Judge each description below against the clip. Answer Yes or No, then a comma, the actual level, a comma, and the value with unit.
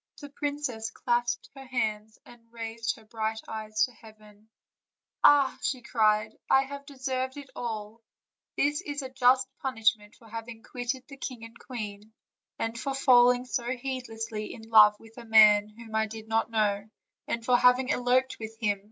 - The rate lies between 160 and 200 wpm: Yes, average, 170 wpm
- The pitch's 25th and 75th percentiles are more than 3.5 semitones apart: No, average, 2.8 semitones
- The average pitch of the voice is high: Yes, high, 230 Hz